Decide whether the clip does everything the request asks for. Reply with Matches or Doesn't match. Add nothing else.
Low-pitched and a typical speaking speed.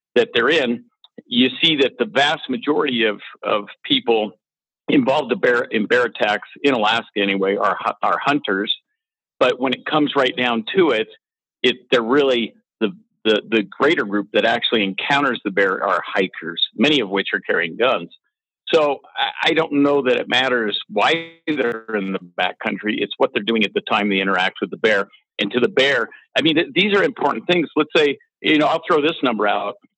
Matches